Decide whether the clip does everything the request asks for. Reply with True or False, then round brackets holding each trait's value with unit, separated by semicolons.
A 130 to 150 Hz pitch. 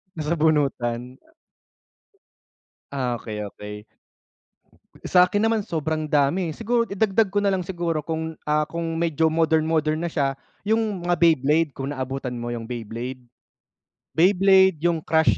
False (160 Hz)